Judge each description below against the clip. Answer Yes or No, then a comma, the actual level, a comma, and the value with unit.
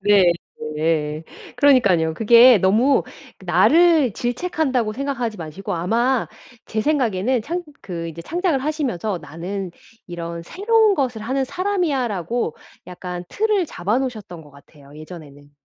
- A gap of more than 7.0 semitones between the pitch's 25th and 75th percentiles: Yes, wide, 8.1 semitones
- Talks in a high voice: Yes, high, 220 Hz